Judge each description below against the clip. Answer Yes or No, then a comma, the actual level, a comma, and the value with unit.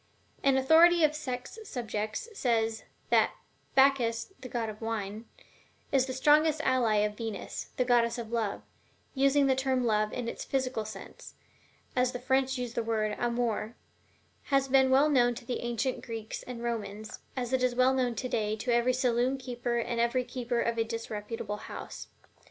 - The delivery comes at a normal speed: Yes, average, 170 wpm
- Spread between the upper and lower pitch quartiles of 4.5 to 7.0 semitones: No, narrow, 2.5 semitones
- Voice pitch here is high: Yes, high, 245 Hz